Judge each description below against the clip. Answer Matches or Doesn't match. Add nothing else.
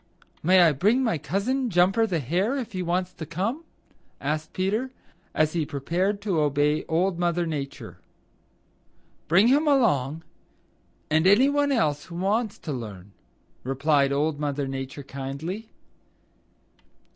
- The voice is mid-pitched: Matches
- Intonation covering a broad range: Matches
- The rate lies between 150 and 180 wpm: Doesn't match